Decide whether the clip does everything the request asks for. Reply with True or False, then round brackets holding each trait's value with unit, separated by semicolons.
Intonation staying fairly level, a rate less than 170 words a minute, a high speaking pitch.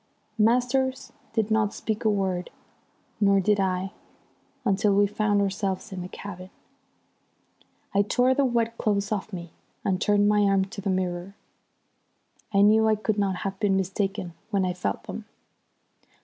True (2.1 semitones; 155 wpm; 200 Hz)